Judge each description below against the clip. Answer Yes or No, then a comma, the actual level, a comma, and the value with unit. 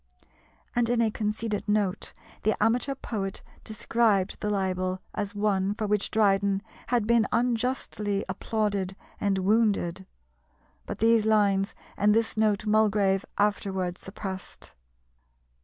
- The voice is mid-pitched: No, high, 210 Hz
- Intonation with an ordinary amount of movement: No, narrow, 2.1 semitones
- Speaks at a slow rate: Yes, slow, 120 wpm